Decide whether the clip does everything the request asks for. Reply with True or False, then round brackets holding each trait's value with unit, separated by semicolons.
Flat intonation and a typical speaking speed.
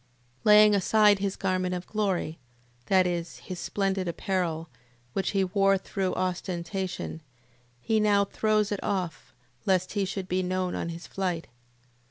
True (1.9 semitones; 145 wpm)